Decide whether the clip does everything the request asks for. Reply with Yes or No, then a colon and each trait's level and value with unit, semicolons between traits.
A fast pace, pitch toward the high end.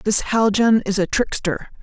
No: average, 165 wpm; high, 210 Hz